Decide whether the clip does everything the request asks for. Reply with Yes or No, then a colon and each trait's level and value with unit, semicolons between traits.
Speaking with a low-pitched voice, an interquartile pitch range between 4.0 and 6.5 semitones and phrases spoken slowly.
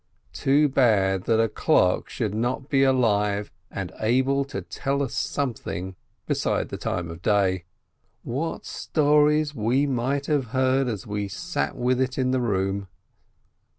No: low, 125 Hz; average, 5.0 semitones; average, 150 wpm